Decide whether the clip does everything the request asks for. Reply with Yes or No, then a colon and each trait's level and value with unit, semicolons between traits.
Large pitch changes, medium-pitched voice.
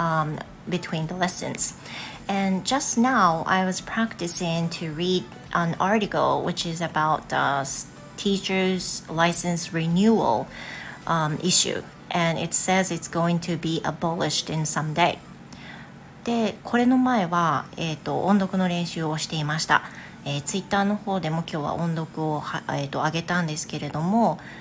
No: average, 3.1 semitones; medium, 170 Hz